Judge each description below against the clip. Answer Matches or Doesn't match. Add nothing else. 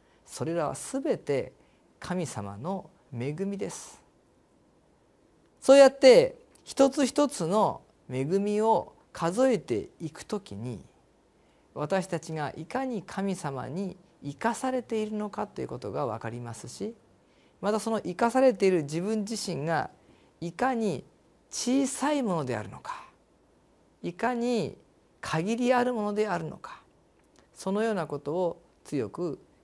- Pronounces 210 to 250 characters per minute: Matches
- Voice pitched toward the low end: Doesn't match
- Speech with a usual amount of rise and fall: Doesn't match